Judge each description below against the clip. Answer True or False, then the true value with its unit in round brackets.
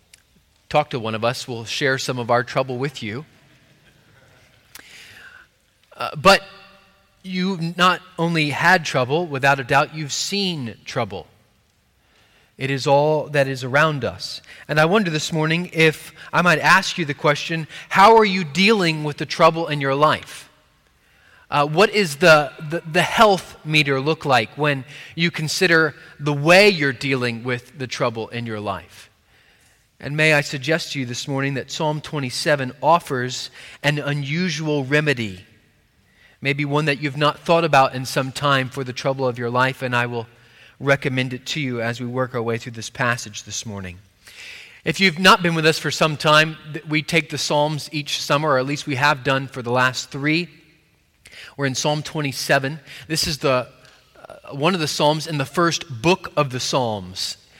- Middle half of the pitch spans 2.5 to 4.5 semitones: True (3.8 semitones)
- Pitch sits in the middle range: True (145 Hz)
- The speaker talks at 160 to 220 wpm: True (175 wpm)